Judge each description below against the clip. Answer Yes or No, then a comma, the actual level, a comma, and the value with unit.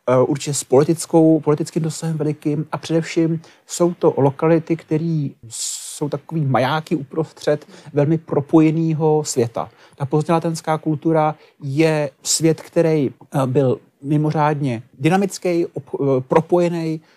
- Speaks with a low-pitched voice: No, medium, 155 Hz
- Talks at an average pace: No, slow, 100 wpm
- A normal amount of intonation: No, narrow, 2.0 semitones